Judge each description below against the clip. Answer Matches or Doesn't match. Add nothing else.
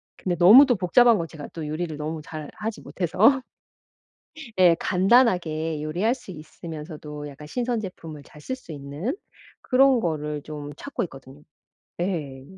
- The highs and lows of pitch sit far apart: Matches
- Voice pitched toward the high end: Doesn't match